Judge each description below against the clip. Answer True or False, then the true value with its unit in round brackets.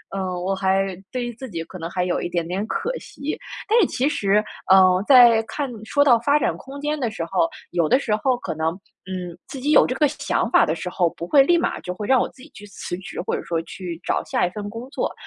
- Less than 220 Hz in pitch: True (210 Hz)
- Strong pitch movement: True (6.7 semitones)